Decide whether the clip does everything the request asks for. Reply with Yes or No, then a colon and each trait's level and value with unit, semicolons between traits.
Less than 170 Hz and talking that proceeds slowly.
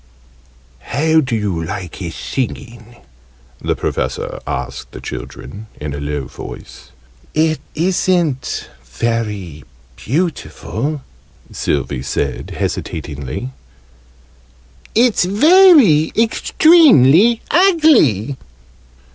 Yes: low, 135 Hz; slow, 80 wpm